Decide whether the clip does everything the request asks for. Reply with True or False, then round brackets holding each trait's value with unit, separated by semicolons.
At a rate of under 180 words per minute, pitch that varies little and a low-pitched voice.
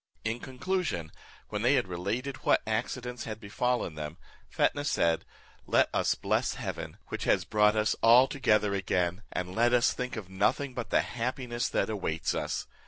False (170 wpm; 4.3 semitones; 110 Hz)